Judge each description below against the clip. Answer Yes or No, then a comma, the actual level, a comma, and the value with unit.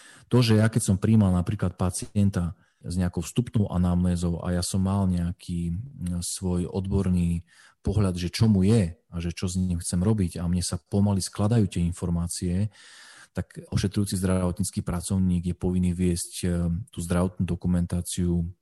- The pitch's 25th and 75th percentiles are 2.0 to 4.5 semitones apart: Yes, narrow, 2.4 semitones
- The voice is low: Yes, very low, 90 Hz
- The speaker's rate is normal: Yes, average, 155 wpm